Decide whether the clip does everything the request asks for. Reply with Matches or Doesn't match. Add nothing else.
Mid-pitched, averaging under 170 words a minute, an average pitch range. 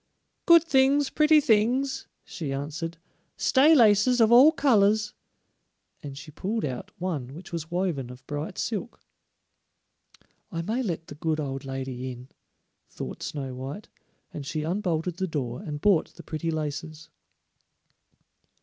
Doesn't match